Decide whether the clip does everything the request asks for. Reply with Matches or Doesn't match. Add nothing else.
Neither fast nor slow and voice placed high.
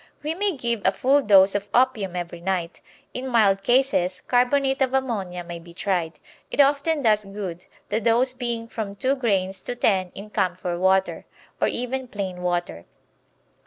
Matches